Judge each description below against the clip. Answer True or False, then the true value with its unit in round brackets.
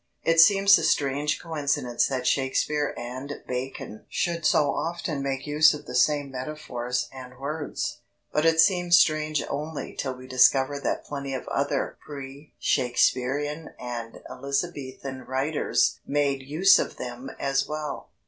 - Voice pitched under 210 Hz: True (140 Hz)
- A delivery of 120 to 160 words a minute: True (140 wpm)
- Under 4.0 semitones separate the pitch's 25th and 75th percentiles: True (2.7 semitones)